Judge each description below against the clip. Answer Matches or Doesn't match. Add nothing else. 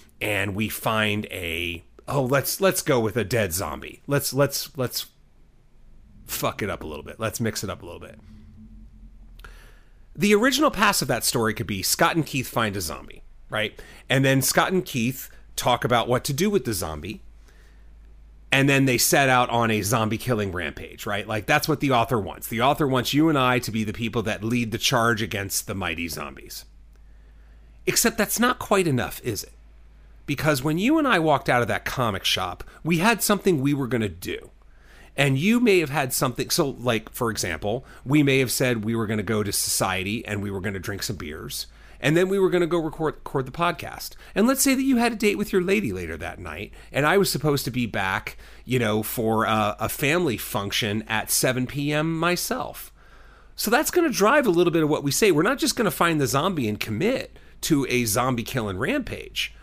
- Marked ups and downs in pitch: Matches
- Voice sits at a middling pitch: Doesn't match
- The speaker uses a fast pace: Matches